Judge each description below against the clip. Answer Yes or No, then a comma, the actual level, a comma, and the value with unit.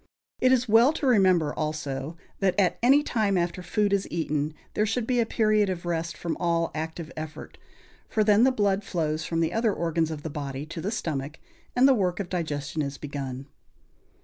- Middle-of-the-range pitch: Yes, medium, 175 Hz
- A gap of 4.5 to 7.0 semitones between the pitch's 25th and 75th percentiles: Yes, wide, 5.4 semitones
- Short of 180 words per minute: No, average, 200 wpm